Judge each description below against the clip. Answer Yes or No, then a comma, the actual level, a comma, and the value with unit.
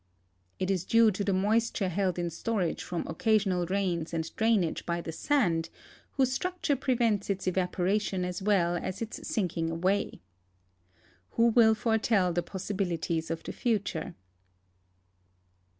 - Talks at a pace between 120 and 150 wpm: Yes, slow, 135 wpm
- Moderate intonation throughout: Yes, average, 4.0 semitones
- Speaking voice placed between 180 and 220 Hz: Yes, high, 190 Hz